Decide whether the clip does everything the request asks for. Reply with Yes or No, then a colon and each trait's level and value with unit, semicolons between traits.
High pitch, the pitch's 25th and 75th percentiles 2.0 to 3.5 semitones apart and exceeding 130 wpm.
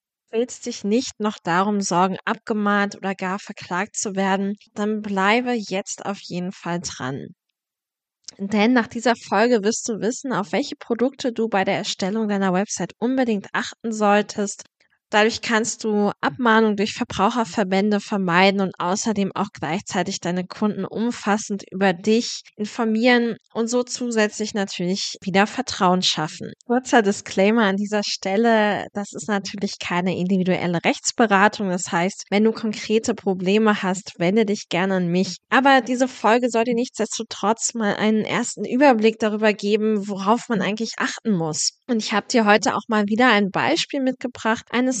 Yes: high, 210 Hz; average, 2.8 semitones; average, 150 wpm